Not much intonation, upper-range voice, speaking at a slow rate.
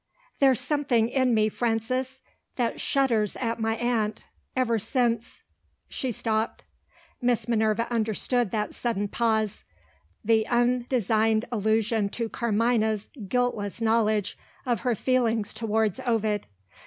Yes: narrow, 2.0 semitones; high, 225 Hz; slow, 115 wpm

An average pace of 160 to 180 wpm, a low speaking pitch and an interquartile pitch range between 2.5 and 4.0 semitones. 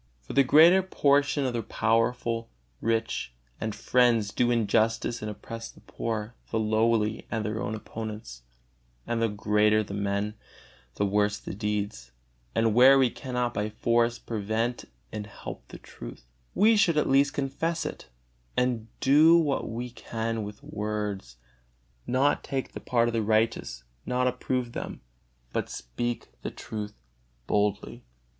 No: average, 150 wpm; low, 115 Hz; average, 3.0 semitones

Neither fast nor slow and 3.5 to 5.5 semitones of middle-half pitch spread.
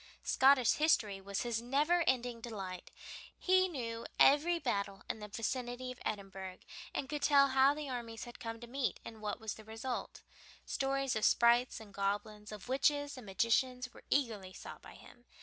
Yes: average, 180 wpm; average, 4.1 semitones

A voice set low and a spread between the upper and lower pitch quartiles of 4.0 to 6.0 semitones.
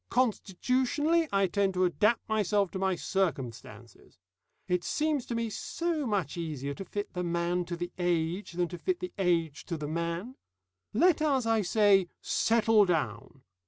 No: high, 190 Hz; average, 5.0 semitones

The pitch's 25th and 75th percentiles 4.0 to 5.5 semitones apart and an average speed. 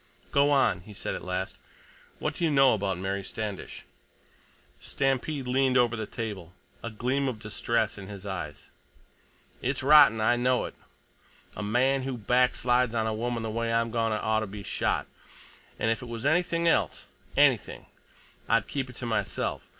No: average, 3.4 semitones; average, 165 wpm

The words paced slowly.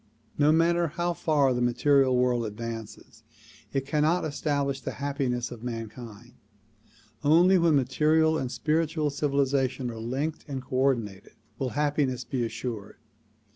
Yes: slow, 130 wpm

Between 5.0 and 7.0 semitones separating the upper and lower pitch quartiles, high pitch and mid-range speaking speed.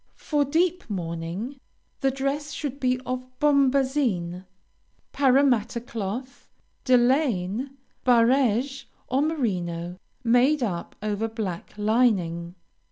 No: wide, 5.5 semitones; high, 245 Hz; slow, 95 wpm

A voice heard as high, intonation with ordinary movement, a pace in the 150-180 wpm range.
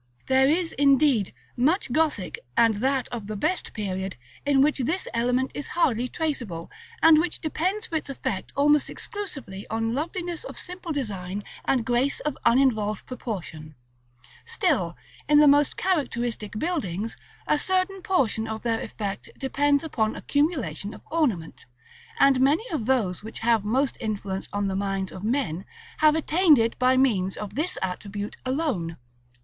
No: very high, 255 Hz; wide, 6.3 semitones; average, 155 wpm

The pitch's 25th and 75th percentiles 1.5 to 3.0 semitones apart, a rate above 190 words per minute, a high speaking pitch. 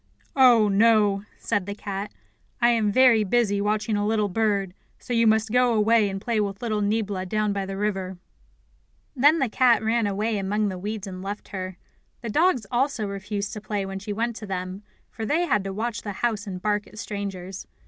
Yes: narrow, 2.4 semitones; average, 200 wpm; high, 210 Hz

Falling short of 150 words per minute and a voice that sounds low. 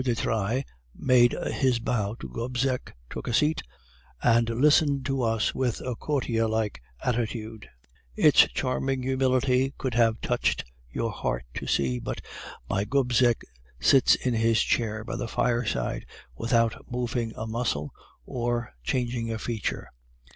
Yes: average, 140 wpm; low, 120 Hz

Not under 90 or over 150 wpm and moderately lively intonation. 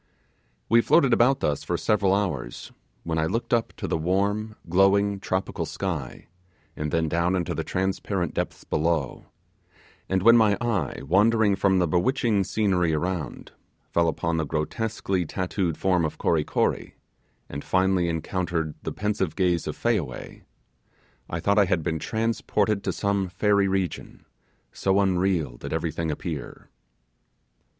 Yes: average, 145 wpm; average, 3.6 semitones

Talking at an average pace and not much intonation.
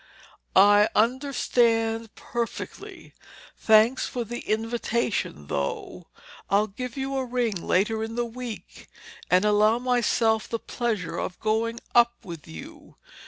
No: slow, 120 wpm; narrow, 2.3 semitones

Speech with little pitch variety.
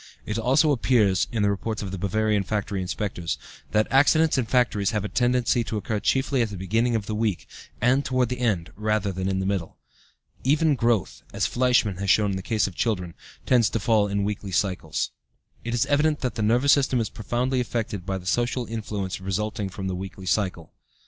No: average, 3.9 semitones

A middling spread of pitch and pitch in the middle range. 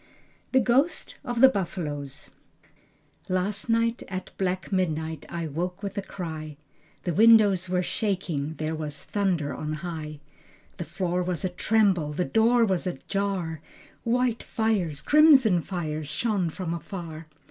Yes: average, 4.8 semitones; medium, 180 Hz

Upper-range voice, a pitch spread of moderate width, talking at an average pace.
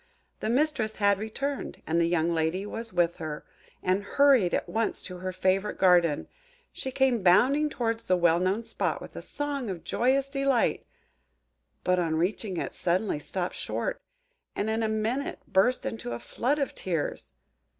No: high, 205 Hz; wide, 6.0 semitones; average, 170 wpm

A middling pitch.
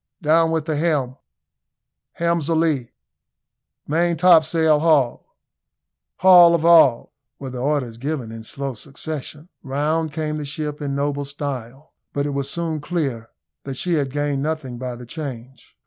Yes: medium, 145 Hz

